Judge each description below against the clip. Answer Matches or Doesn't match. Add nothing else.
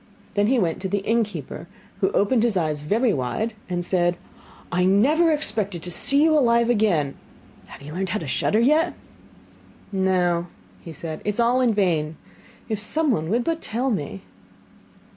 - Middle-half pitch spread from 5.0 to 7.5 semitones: Matches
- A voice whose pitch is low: Doesn't match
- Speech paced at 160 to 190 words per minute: Matches